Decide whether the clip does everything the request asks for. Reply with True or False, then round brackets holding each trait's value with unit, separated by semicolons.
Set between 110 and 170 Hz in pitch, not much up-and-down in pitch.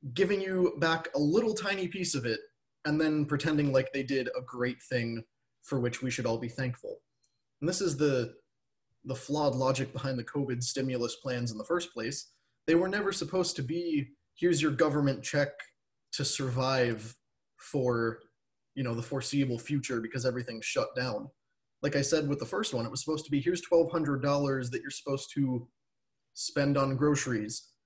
False (135 Hz; 3.4 semitones)